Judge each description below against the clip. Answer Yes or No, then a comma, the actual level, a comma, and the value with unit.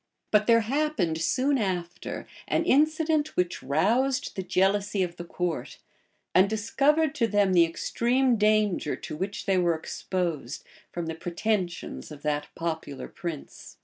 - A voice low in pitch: No, high, 190 Hz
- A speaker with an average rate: Yes, average, 145 wpm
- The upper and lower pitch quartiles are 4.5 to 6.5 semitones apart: Yes, wide, 5.6 semitones